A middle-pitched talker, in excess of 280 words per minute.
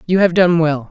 No: medium, 170 Hz; fast, 265 wpm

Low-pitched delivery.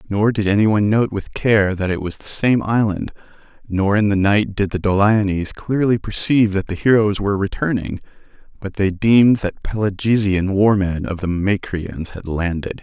Yes: low, 100 Hz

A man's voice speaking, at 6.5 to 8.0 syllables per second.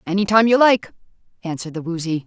No: female; 6.7 syllables/s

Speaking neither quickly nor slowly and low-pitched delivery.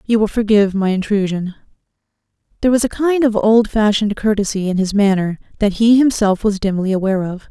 No: average, 175 wpm; high, 205 Hz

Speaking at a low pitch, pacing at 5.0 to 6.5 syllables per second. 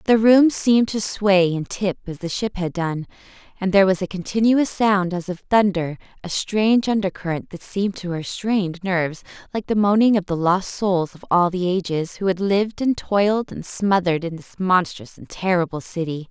No: high, 190 Hz; 5.1 syllables/s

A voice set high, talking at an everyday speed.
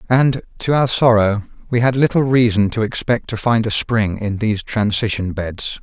No: low, 110 Hz; average, 185 wpm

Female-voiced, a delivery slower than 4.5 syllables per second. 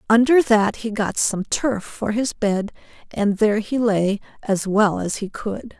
Yes: female; 4.0 syllables/s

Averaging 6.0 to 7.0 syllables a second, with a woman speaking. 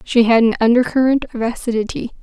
Yes: 6.1 syllables/s; female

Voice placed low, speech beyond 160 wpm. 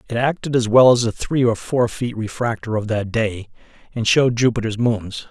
Yes: low, 115 Hz; fast, 205 wpm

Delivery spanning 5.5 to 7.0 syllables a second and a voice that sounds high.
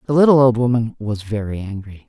No: 5.9 syllables/s; low, 120 Hz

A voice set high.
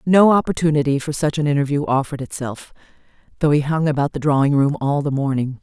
No: medium, 145 Hz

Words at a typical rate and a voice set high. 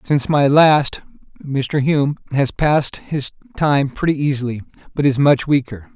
No: average, 150 wpm; medium, 140 Hz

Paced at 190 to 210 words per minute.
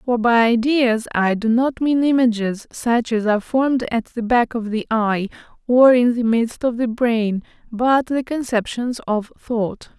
No: average, 180 wpm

